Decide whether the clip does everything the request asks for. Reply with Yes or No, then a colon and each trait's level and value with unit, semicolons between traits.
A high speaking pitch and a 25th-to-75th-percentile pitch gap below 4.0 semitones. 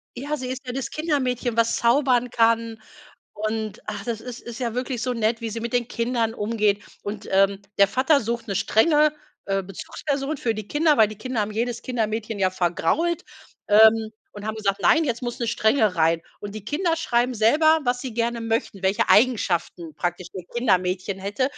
Yes: high, 230 Hz; average, 3.4 semitones